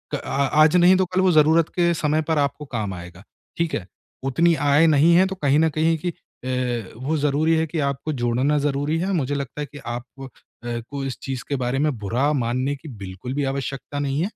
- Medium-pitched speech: Yes, medium, 145 Hz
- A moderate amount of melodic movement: Yes, average, 3.7 semitones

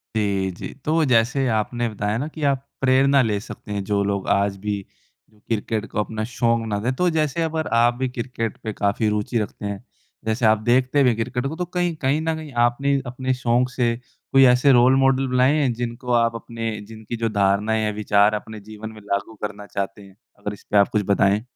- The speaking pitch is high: No, low, 115 Hz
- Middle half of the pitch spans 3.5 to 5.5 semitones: Yes, average, 3.8 semitones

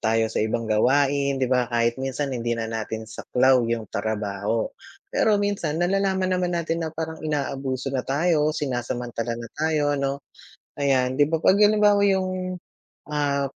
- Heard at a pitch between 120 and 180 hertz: Yes, medium, 140 Hz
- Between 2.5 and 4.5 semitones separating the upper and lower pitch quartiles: No, wide, 5.6 semitones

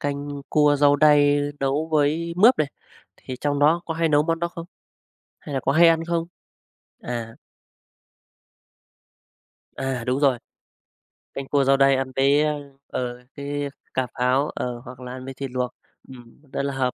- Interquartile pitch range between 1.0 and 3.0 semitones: Yes, narrow, 2.5 semitones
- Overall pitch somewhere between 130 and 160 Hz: Yes, medium, 140 Hz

